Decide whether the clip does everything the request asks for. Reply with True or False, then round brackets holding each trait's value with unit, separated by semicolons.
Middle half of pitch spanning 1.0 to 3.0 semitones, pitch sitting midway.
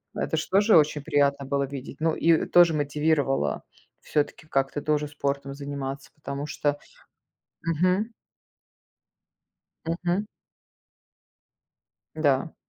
True (2.6 semitones; 145 Hz)